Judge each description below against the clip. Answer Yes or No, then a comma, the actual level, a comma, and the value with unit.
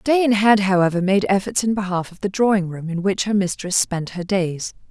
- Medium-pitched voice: No, high, 195 Hz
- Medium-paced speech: No, fast, 220 wpm